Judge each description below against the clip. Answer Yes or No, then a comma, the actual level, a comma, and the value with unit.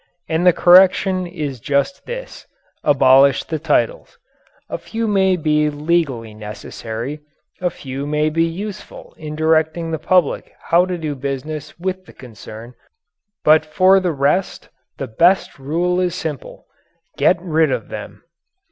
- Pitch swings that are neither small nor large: Yes, average, 4.3 semitones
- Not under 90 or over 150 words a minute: Yes, average, 140 wpm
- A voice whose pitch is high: No, medium, 160 Hz